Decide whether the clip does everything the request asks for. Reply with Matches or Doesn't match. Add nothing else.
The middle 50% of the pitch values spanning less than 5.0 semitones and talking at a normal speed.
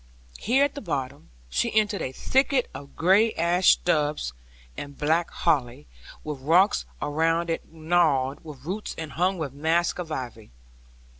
Matches